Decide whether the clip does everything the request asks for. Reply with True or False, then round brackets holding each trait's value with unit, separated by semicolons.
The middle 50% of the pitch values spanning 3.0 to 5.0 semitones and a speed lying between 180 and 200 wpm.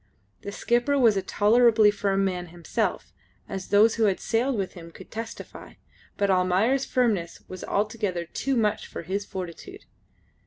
False (3.8 semitones; 155 wpm)